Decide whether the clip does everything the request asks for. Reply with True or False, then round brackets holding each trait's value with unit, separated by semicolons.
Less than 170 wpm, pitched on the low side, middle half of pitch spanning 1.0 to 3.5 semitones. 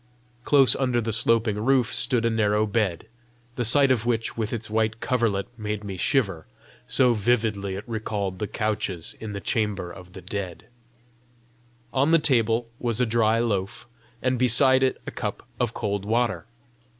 True (160 wpm; 110 Hz; 2.9 semitones)